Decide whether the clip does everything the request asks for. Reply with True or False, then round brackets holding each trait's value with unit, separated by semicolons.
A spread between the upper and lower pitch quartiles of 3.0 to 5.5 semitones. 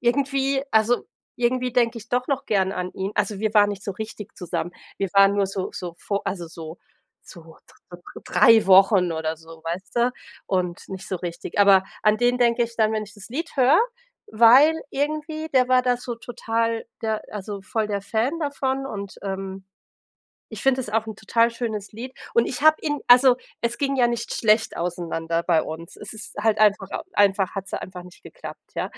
True (4.3 semitones)